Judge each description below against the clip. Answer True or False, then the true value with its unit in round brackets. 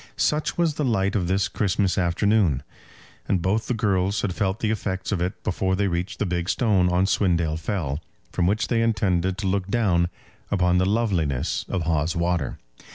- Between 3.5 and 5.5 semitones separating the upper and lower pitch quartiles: False (3.0 semitones)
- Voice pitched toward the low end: True (95 Hz)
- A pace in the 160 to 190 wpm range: True (185 wpm)